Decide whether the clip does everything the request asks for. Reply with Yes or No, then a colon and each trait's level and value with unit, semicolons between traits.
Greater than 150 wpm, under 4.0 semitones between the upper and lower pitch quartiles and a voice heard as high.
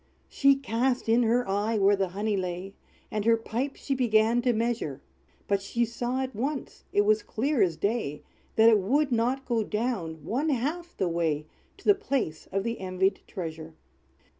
No: average, 180 wpm; average, 4.3 semitones; high, 225 Hz